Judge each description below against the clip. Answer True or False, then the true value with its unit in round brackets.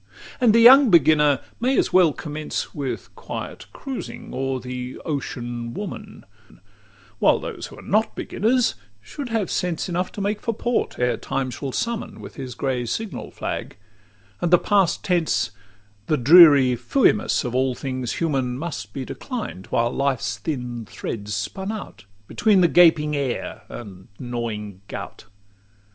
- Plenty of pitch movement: True (7.7 semitones)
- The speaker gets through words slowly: False (150 wpm)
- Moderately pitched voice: True (145 Hz)